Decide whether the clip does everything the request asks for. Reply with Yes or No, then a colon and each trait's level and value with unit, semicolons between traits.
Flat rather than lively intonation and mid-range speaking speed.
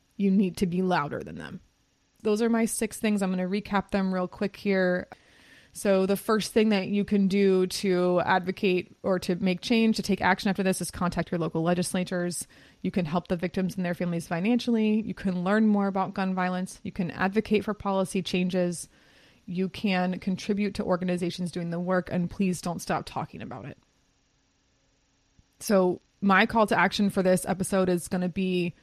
Yes: narrow, 2.0 semitones; average, 195 wpm